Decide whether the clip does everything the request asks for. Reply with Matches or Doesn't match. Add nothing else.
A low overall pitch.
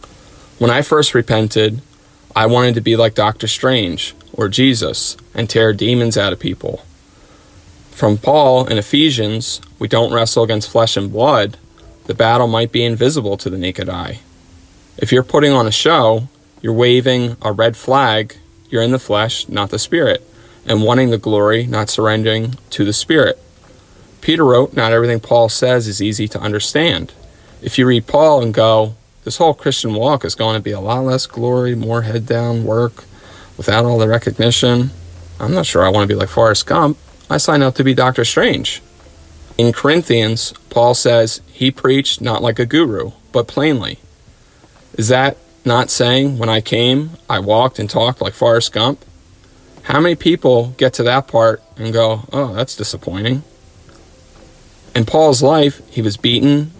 Matches